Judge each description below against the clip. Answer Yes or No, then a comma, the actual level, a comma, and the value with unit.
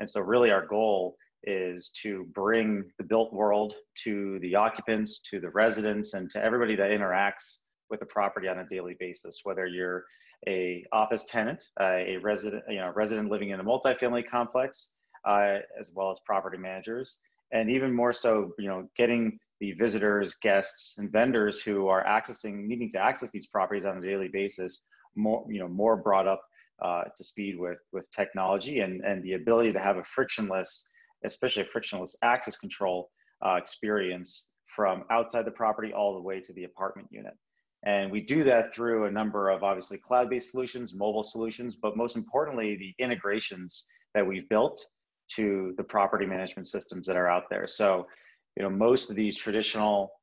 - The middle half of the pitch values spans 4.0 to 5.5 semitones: No, average, 2.9 semitones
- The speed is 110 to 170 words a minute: No, average, 180 wpm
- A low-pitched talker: Yes, low, 105 Hz